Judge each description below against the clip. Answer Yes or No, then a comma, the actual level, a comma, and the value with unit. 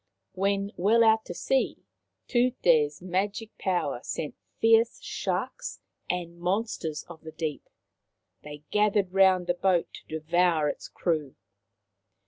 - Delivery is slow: Yes, slow, 120 wpm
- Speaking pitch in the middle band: Yes, medium, 180 Hz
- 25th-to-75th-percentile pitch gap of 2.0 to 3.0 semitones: No, average, 4.3 semitones